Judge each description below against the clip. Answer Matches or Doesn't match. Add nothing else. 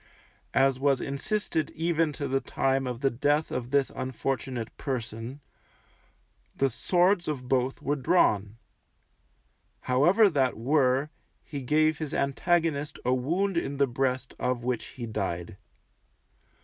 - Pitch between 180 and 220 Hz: Doesn't match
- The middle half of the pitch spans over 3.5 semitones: Doesn't match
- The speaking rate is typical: Doesn't match